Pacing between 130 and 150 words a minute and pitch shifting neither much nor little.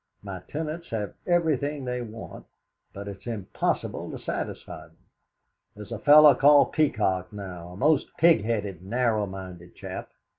No: average, 140 wpm; wide, 7.0 semitones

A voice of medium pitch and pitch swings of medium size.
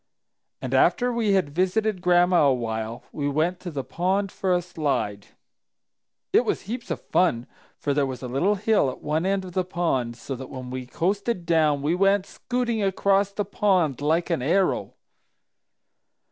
No: medium, 175 Hz; wide, 5.9 semitones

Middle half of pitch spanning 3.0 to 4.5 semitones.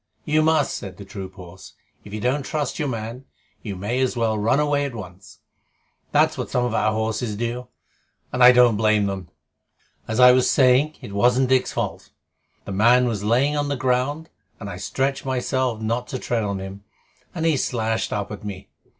Yes: average, 3.8 semitones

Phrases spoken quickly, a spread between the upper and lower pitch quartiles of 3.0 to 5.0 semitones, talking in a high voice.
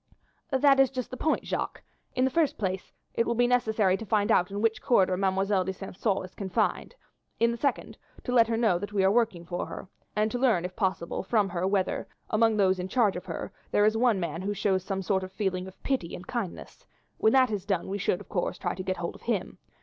Yes: fast, 245 wpm; average, 3.7 semitones; high, 200 Hz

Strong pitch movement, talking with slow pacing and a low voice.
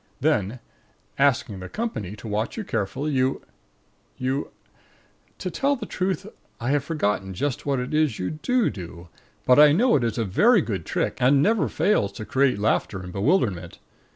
No: wide, 7.2 semitones; average, 180 wpm; low, 130 Hz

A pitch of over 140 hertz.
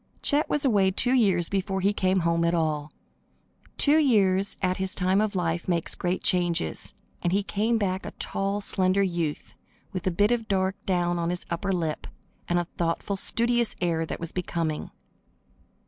Yes: medium, 185 Hz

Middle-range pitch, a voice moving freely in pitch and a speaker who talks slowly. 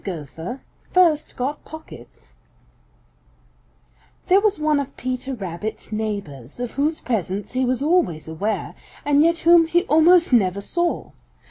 No: very high, 255 Hz; wide, 8.2 semitones; slow, 130 wpm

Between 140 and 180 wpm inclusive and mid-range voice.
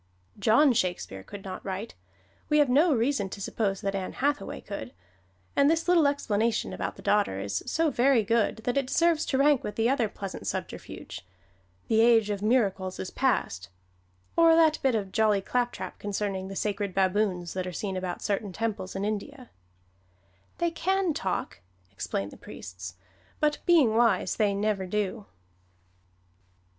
No: average, 160 wpm; high, 215 Hz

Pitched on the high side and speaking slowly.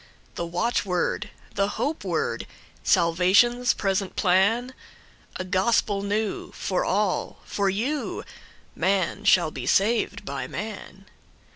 Yes: high, 195 Hz; slow, 90 wpm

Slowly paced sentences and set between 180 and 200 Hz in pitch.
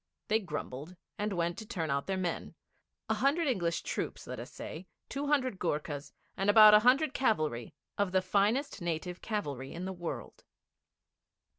No: average, 165 wpm; high, 190 Hz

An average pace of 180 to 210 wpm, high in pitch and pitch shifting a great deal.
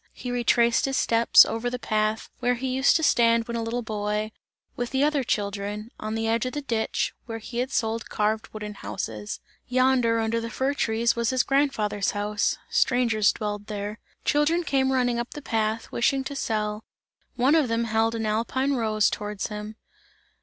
No: average, 185 wpm; high, 230 Hz; average, 3.0 semitones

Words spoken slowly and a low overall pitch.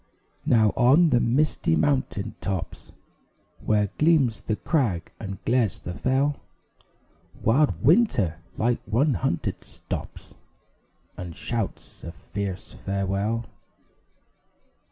Yes: slow, 100 wpm; low, 115 Hz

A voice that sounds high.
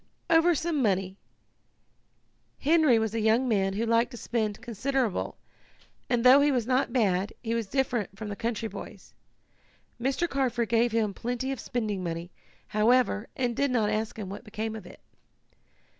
Yes: high, 230 Hz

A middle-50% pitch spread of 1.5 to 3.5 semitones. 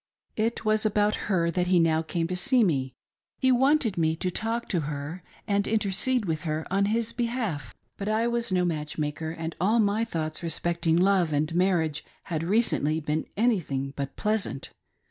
No: wide, 5.4 semitones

